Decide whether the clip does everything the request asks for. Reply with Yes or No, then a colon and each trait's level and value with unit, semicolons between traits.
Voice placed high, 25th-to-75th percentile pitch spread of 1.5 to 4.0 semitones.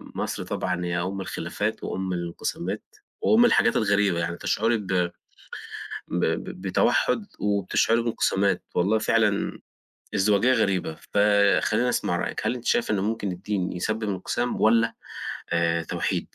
No: low, 100 Hz; average, 3.7 semitones